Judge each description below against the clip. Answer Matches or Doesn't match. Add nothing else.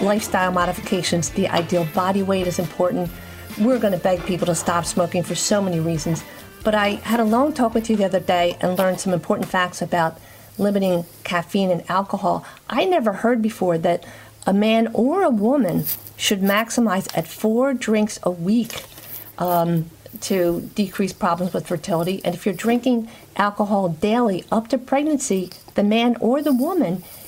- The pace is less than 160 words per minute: Doesn't match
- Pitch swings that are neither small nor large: Matches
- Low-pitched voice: Doesn't match